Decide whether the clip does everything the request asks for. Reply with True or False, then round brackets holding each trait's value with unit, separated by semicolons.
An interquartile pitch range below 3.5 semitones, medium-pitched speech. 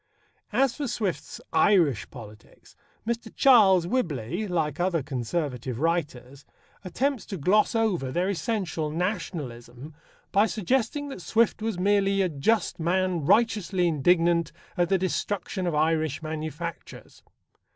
False (5.2 semitones; 175 Hz)